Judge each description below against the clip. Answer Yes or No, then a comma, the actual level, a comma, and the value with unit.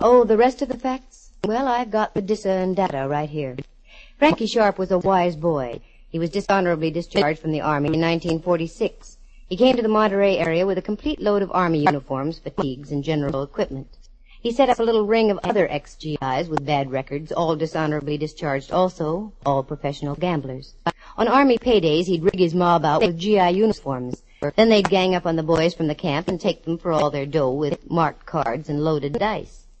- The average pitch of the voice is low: No, medium, 170 Hz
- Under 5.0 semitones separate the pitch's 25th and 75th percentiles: No, wide, 5.6 semitones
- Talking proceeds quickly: Yes, fast, 210 wpm